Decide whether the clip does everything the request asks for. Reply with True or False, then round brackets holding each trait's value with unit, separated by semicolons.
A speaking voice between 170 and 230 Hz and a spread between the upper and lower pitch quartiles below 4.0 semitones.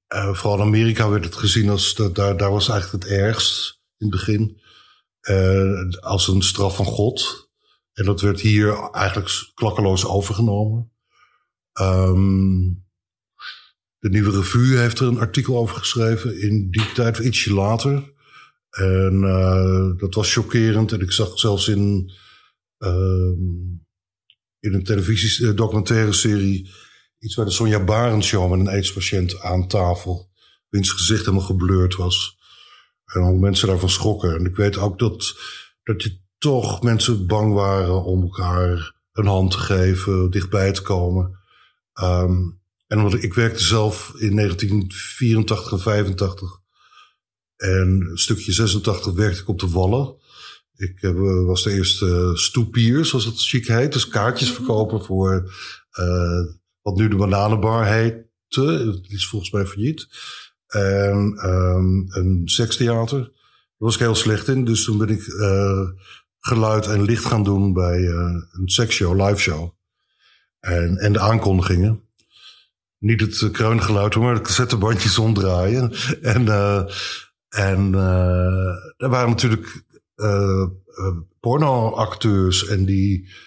False (100 Hz; 2.9 semitones)